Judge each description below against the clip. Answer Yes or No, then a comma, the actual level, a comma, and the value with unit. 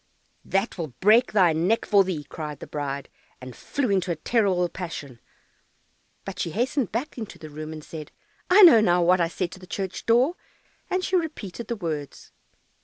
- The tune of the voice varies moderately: No, wide, 6.4 semitones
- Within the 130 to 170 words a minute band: No, average, 185 wpm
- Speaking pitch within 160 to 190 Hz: Yes, medium, 185 Hz